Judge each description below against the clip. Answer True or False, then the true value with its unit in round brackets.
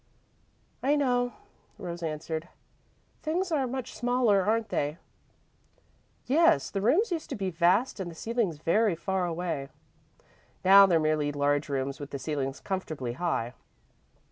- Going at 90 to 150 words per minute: True (140 wpm)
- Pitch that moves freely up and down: True (7.9 semitones)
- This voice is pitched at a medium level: True (180 Hz)